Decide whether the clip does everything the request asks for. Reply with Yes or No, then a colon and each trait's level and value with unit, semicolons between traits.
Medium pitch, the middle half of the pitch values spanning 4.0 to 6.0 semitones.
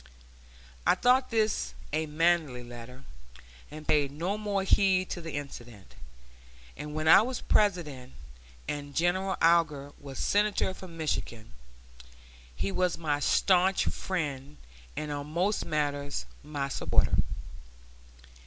Yes: medium, 155 Hz; average, 4.6 semitones